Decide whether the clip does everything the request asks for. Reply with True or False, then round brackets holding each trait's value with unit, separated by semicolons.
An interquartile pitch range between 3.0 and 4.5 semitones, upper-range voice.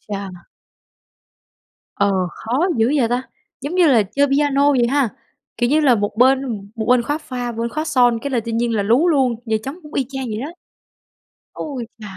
True (3.6 semitones; 250 Hz)